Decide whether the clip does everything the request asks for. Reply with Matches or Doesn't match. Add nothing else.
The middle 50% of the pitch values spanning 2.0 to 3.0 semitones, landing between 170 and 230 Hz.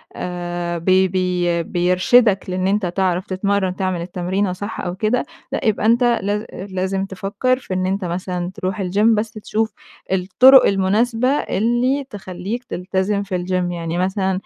Matches